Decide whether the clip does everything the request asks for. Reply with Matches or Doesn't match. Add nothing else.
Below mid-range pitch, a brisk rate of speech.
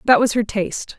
Doesn't match